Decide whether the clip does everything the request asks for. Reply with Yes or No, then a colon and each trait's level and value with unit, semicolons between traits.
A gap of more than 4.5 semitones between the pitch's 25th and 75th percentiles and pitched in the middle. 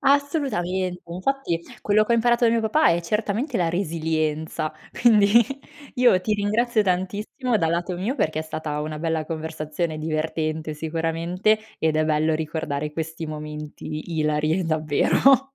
Yes: average, 5.3 semitones; medium, 165 Hz